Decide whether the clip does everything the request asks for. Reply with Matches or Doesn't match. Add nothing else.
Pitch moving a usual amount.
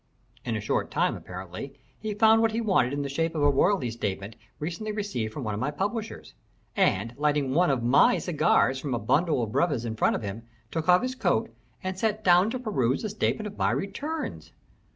Doesn't match